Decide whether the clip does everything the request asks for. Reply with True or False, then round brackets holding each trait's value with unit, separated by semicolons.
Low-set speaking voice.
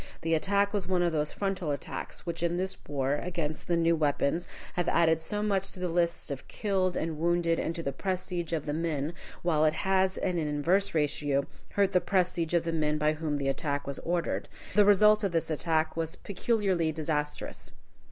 False (165 Hz)